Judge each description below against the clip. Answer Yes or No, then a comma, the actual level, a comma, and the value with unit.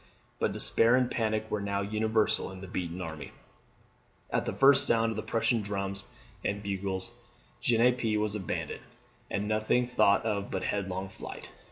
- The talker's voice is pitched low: Yes, low, 105 Hz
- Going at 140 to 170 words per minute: Yes, average, 160 wpm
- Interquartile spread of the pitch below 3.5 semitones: Yes, narrow, 2.6 semitones